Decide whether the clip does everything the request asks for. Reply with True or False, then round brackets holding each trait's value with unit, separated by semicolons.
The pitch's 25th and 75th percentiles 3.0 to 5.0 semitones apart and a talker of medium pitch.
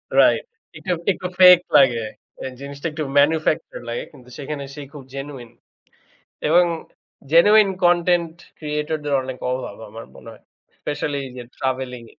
True (4.5 semitones; 145 Hz)